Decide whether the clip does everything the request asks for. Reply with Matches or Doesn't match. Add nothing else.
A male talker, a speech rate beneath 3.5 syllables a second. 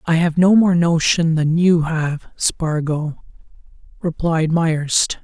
Matches